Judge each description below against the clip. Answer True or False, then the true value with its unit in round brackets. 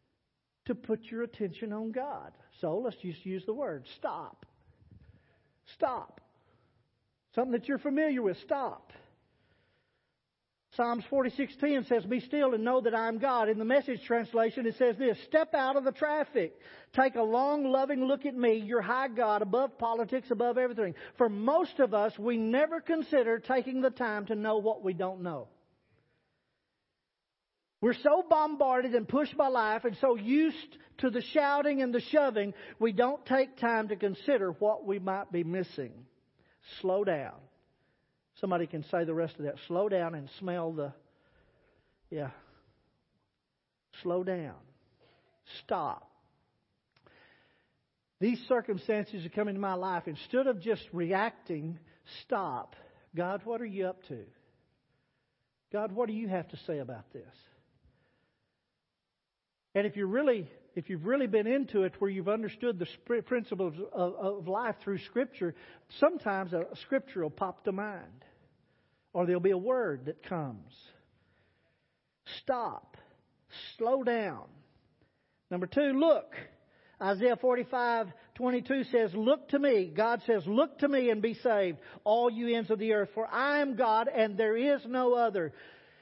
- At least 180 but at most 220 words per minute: False (150 wpm)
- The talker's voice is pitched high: True (225 Hz)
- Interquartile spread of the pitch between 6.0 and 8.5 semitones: False (5.1 semitones)